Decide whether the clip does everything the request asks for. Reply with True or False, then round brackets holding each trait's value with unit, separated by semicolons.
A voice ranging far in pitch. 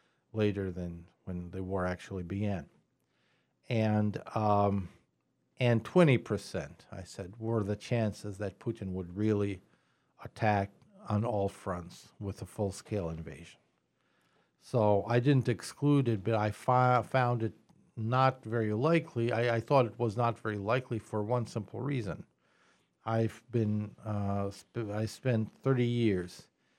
False (3.2 semitones)